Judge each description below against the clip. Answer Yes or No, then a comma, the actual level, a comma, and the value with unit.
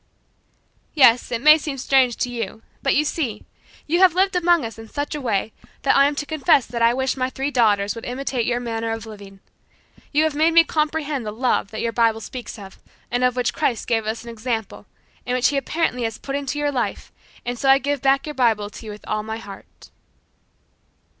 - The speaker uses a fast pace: Yes, fast, 225 wpm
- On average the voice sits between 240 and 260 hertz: Yes, very high, 250 Hz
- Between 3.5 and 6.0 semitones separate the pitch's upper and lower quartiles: Yes, average, 4.1 semitones